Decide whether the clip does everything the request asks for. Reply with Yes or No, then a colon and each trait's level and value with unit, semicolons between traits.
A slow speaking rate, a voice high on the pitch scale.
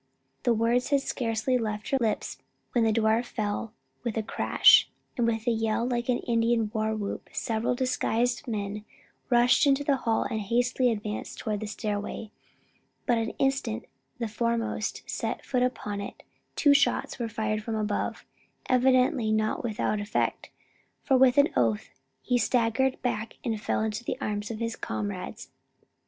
No: average, 160 wpm; high, 230 Hz